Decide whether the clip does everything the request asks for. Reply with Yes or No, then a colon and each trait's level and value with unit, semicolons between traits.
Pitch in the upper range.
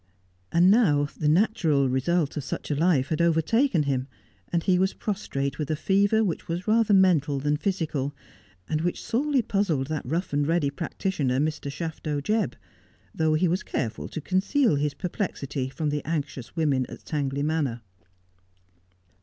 No: medium, 155 Hz